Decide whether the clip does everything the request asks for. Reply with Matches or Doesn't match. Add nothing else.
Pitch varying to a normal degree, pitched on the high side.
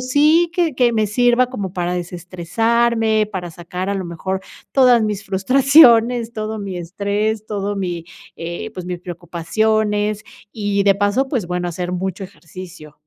Matches